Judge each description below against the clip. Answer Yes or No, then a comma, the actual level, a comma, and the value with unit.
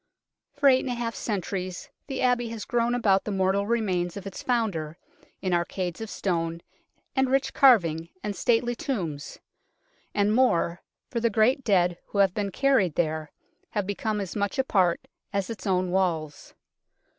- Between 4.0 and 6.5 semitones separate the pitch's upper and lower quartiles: Yes, average, 4.9 semitones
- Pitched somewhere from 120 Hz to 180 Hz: No, high, 200 Hz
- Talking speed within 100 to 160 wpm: No, average, 170 wpm